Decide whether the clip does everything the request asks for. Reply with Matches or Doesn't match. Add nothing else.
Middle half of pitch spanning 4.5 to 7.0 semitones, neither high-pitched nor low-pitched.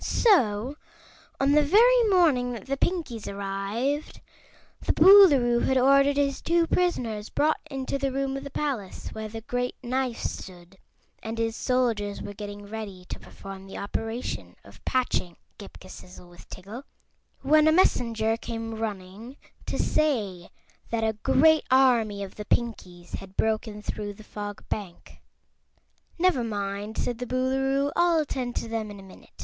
Doesn't match